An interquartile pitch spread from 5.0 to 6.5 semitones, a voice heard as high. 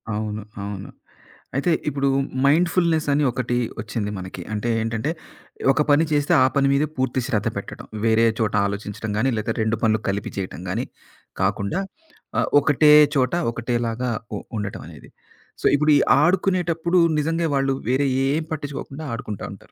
No: wide, 5.6 semitones; low, 130 Hz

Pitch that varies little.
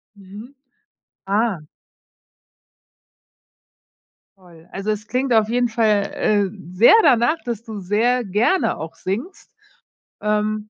No: average, 3.1 semitones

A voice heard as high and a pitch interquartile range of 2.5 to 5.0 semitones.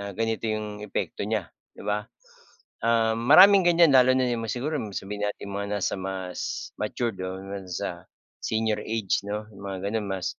No: low, 105 Hz; average, 2.8 semitones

